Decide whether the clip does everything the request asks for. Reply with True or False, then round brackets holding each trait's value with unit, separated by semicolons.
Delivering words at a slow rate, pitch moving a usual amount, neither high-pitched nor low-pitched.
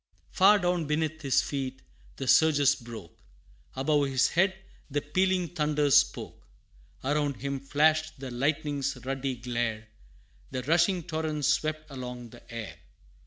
True (130 wpm; 3.3 semitones; 145 Hz)